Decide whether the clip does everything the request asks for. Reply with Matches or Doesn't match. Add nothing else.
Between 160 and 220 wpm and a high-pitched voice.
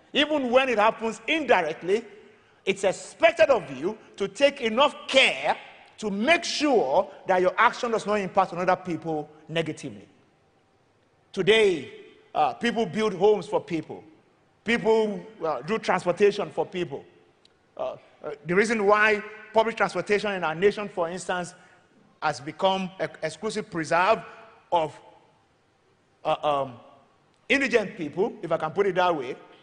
Doesn't match